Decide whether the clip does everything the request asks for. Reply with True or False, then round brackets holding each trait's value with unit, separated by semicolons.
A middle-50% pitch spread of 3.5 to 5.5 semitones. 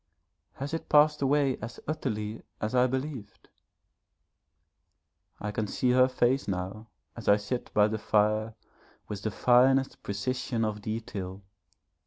True (3.8 semitones)